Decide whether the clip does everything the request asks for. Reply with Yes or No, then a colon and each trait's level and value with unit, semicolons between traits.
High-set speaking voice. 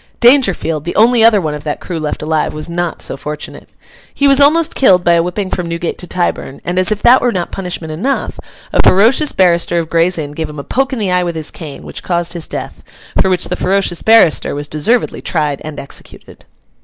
No: medium, 175 Hz